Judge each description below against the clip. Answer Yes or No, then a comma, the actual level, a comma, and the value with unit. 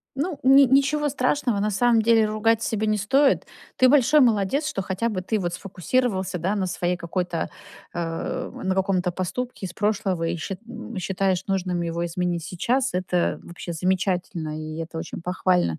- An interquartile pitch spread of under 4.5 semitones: No, average, 4.8 semitones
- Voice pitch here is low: No, high, 190 Hz